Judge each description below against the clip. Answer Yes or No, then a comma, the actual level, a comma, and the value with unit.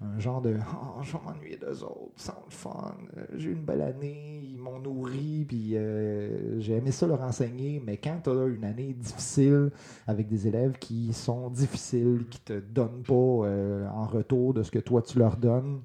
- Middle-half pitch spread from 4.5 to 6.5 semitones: No, average, 3.2 semitones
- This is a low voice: Yes, low, 125 Hz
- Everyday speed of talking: Yes, average, 200 wpm